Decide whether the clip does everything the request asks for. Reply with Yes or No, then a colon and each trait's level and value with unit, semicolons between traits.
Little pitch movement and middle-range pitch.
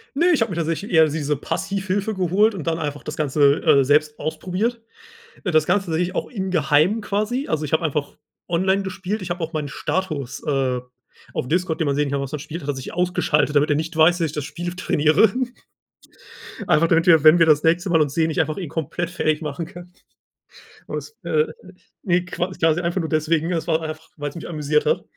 No: average, 3.3 semitones; medium, 165 Hz